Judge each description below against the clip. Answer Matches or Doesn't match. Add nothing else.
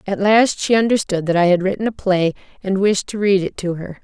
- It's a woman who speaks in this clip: Matches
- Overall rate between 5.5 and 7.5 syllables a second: Matches